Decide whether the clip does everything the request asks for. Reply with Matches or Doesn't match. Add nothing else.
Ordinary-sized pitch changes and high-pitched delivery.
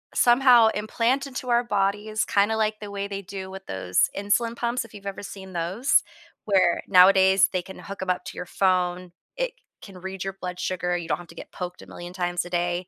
Matches